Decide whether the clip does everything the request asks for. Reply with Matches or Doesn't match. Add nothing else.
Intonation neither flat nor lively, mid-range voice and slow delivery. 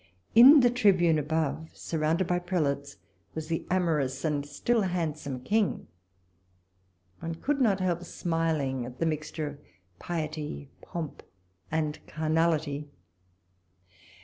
Matches